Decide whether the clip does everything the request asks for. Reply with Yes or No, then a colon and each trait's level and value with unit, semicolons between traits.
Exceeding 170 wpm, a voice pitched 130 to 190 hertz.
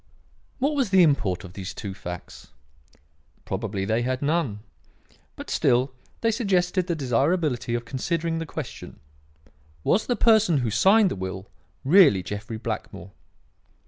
No: average, 140 wpm; medium, 140 Hz